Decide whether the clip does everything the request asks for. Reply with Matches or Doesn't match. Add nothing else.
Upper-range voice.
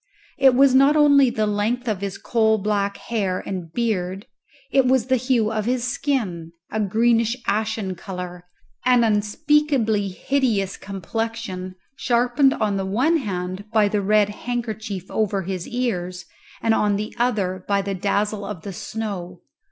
Matches